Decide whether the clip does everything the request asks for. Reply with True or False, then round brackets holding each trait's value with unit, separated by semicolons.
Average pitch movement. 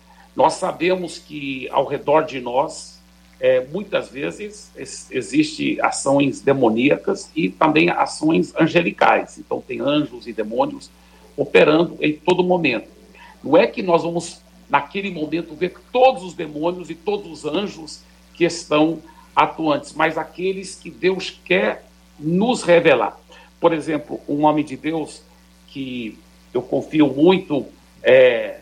True (4.7 semitones)